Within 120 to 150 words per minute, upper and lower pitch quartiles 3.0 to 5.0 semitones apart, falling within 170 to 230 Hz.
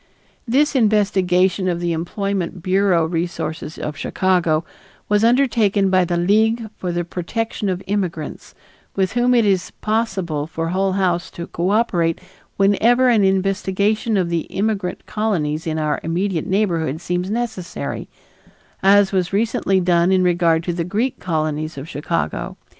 Yes: average, 140 wpm; average, 3.3 semitones; medium, 185 Hz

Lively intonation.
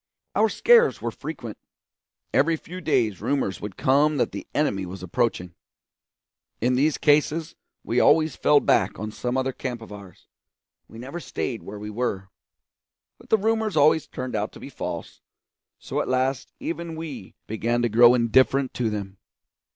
Yes: wide, 5.9 semitones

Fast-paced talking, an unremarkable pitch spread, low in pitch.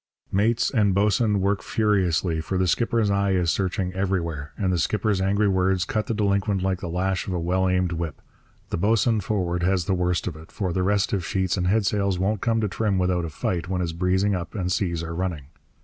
No: fast, 215 wpm; narrow, 2.3 semitones; very low, 95 Hz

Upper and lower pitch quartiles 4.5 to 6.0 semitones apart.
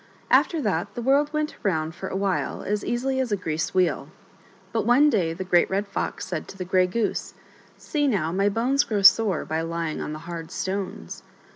Yes: wide, 5.4 semitones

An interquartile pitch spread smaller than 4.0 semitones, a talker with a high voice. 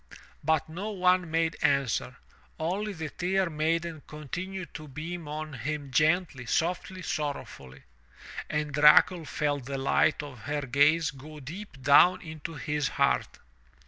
No: average, 3.1 semitones; medium, 155 Hz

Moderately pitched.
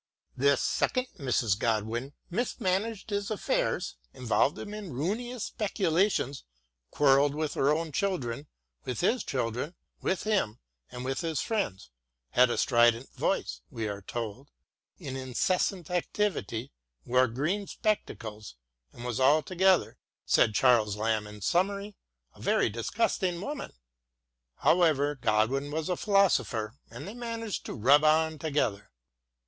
Yes: medium, 145 Hz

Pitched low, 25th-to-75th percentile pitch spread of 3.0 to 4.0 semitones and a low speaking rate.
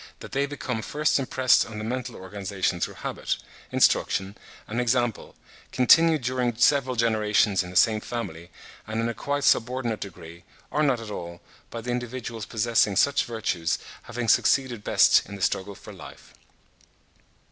No: low, 115 Hz; average, 3.7 semitones; average, 160 wpm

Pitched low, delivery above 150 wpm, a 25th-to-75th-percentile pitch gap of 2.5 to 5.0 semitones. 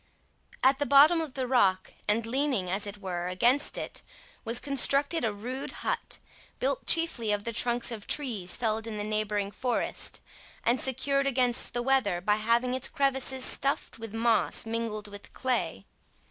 No: high, 235 Hz; average, 165 wpm; average, 4.2 semitones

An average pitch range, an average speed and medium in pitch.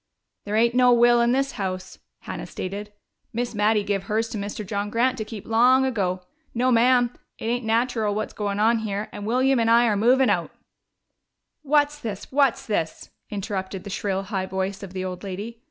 No: average, 3.3 semitones; average, 195 wpm; high, 220 Hz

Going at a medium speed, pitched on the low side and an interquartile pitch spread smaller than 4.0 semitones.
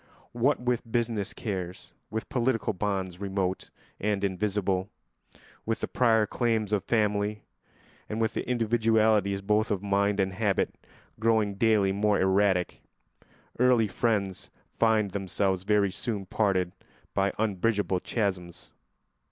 No: slow, 120 wpm; low, 105 Hz; narrow, 2.4 semitones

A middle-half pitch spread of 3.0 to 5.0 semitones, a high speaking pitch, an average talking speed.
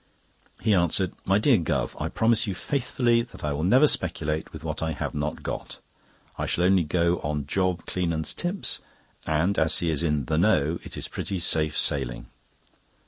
No: average, 4.3 semitones; very low, 85 Hz; average, 185 wpm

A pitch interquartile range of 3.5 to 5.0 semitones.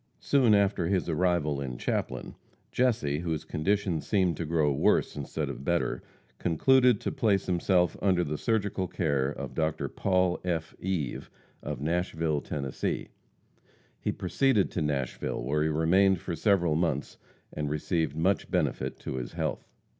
Yes: average, 4.1 semitones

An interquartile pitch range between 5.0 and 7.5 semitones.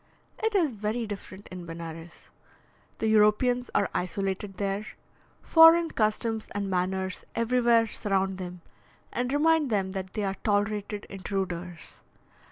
No: average, 3.5 semitones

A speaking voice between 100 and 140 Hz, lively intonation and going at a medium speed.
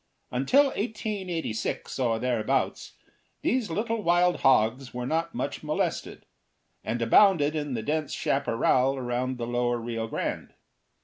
No: low, 135 Hz; wide, 6.3 semitones; slow, 125 wpm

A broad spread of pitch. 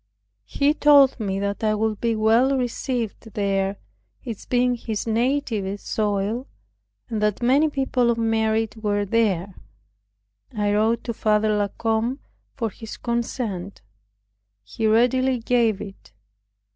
No: average, 2.8 semitones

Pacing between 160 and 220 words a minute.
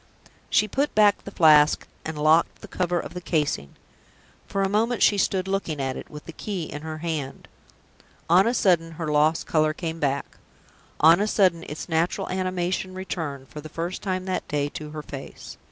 Yes: average, 190 wpm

